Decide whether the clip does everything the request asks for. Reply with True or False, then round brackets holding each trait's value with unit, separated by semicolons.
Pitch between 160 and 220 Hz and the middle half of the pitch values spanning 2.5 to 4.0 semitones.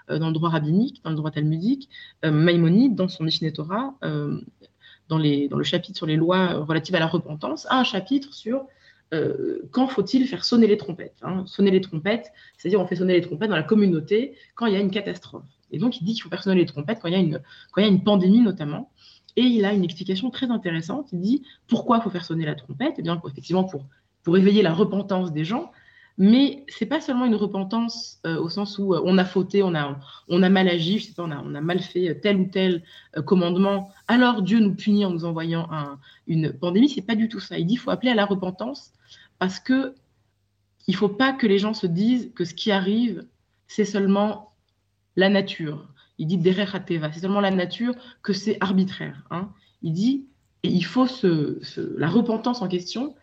False (190 Hz; 4.9 semitones)